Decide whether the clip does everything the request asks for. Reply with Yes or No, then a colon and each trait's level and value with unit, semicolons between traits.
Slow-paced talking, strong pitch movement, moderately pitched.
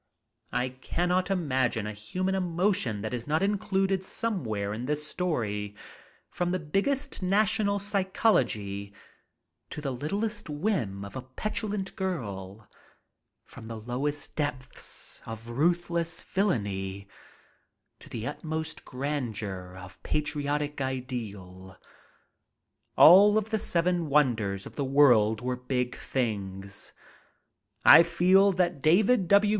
Yes: slow, 115 wpm; wide, 8.9 semitones; medium, 145 Hz